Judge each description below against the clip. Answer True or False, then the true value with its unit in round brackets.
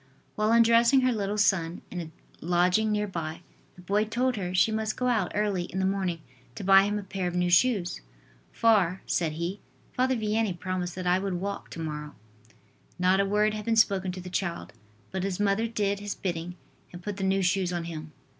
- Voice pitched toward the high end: True (195 Hz)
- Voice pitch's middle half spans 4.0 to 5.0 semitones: False (3.0 semitones)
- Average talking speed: False (210 wpm)